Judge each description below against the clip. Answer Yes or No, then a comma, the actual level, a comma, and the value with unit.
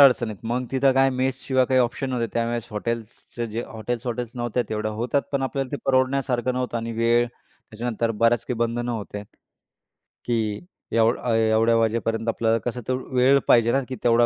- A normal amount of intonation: No, narrow, 2.0 semitones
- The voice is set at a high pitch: No, low, 120 Hz